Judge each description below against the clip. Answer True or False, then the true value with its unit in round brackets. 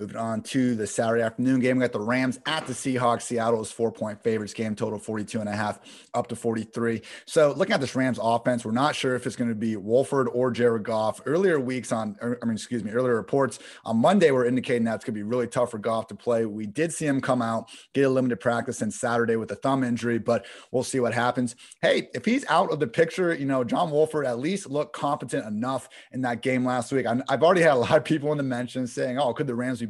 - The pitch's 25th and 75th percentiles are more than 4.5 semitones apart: False (2.4 semitones)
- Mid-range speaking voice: False (120 Hz)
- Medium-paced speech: False (255 wpm)